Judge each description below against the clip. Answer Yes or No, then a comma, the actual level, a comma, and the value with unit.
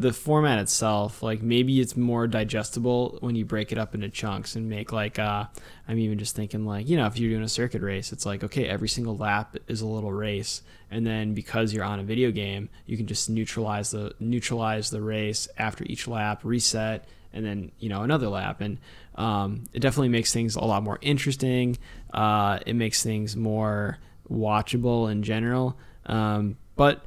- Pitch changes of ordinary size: No, narrow, 1.9 semitones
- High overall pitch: No, low, 110 Hz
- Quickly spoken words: No, average, 195 wpm